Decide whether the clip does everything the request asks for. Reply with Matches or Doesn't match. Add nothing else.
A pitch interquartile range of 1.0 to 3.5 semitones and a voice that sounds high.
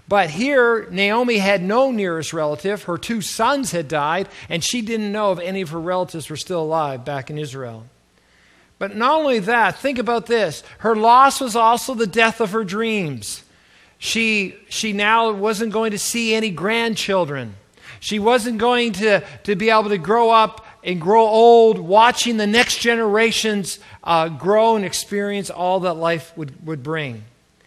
Doesn't match